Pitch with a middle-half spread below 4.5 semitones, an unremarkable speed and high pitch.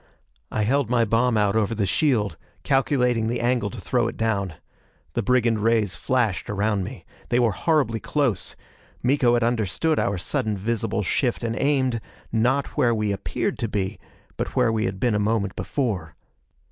No: average, 3.2 semitones; average, 170 wpm; low, 115 Hz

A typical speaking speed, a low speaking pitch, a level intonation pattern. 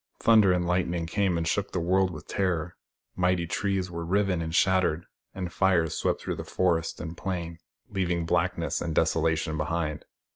Yes: average, 160 wpm; very low, 85 Hz; narrow, 2.1 semitones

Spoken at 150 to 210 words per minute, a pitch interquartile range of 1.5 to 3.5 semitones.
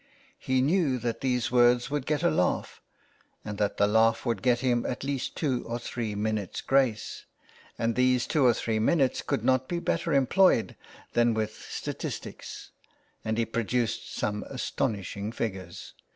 Yes: average, 160 wpm; average, 3.0 semitones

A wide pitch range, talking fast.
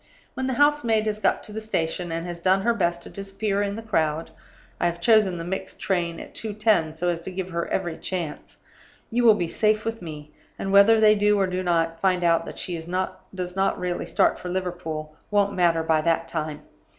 No: average, 3.7 semitones; fast, 220 wpm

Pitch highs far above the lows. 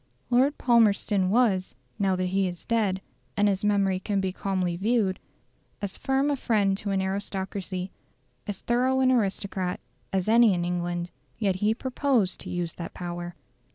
No: average, 3.3 semitones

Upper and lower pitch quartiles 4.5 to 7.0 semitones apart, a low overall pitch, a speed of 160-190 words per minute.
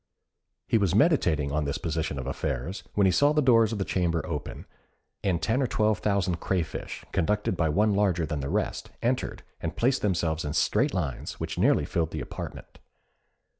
Yes: average, 5.2 semitones; very low, 90 Hz; average, 185 wpm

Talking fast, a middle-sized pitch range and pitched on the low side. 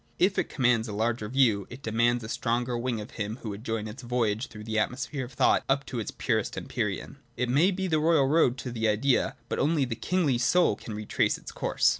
Yes: fast, 235 wpm; average, 3.6 semitones; low, 120 Hz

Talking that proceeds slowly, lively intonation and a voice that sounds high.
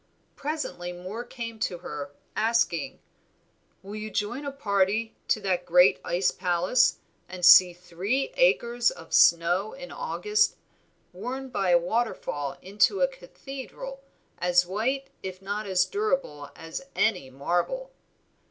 Yes: slow, 130 wpm; wide, 7.0 semitones; high, 205 Hz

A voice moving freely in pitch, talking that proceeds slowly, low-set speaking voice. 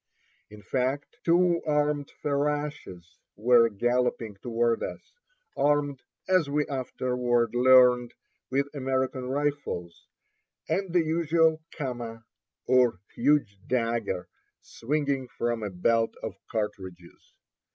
No: average, 4.1 semitones; slow, 100 wpm; low, 130 Hz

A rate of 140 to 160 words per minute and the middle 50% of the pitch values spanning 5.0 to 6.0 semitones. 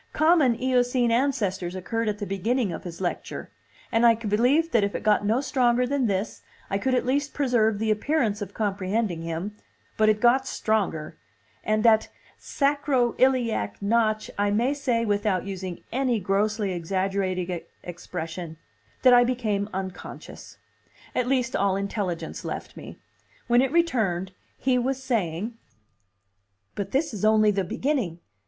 No: average, 150 wpm; average, 4.4 semitones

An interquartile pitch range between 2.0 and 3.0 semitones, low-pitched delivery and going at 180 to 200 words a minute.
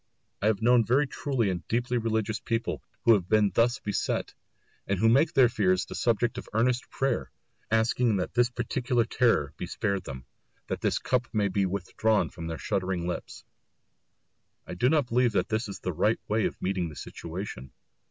No: average, 4.2 semitones; low, 110 Hz; average, 190 wpm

